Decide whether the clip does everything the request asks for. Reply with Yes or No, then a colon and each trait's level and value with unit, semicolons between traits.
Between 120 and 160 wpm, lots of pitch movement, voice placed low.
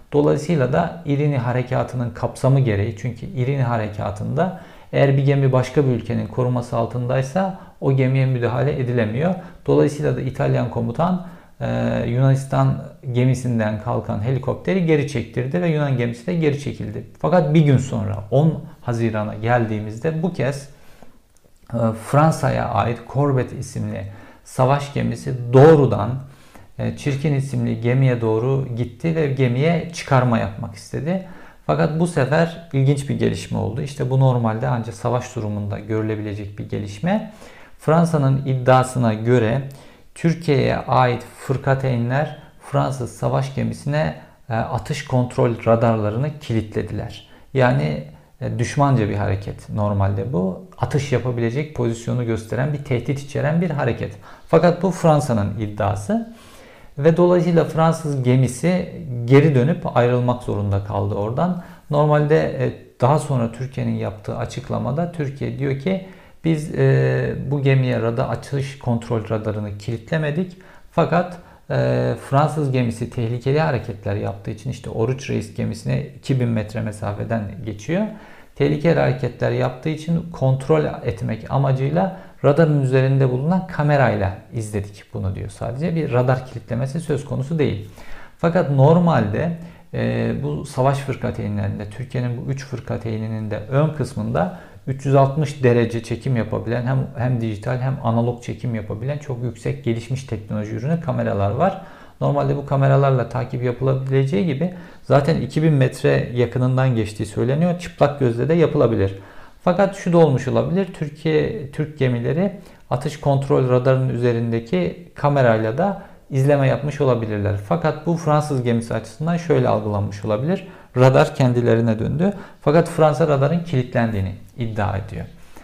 No: average, 125 wpm; average, 4.4 semitones; low, 130 Hz